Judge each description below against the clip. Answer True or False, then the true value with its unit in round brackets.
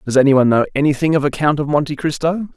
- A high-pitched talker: False (145 Hz)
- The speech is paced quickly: True (260 wpm)